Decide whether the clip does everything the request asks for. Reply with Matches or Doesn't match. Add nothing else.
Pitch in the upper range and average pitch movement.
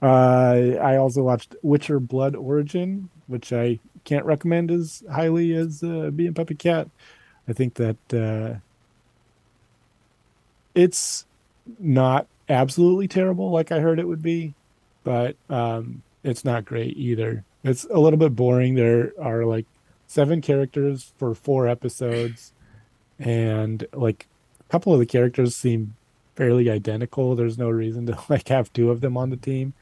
Doesn't match